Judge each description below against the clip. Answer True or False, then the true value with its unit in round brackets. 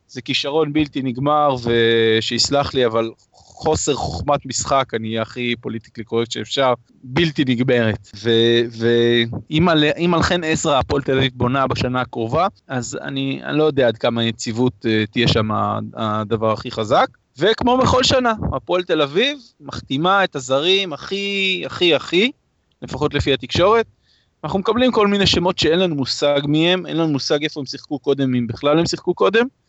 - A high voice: False (135 Hz)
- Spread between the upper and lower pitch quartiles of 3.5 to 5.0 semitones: False (5.4 semitones)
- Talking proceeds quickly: True (160 wpm)